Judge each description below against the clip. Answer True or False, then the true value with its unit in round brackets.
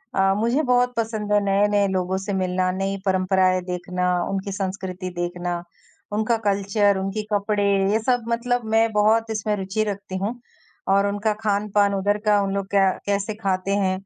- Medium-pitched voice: False (200 Hz)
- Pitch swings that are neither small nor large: False (2.1 semitones)